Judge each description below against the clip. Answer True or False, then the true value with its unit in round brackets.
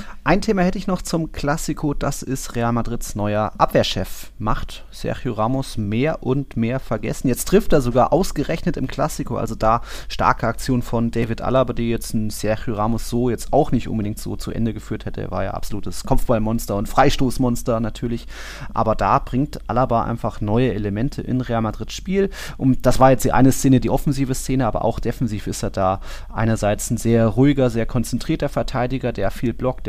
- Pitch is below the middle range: True (120 Hz)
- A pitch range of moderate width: True (3.3 semitones)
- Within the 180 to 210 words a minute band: True (190 wpm)